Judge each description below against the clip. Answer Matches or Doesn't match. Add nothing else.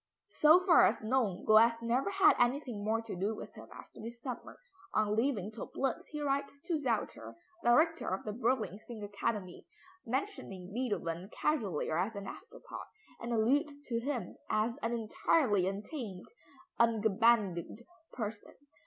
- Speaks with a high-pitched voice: Matches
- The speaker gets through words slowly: Doesn't match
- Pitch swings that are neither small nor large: Matches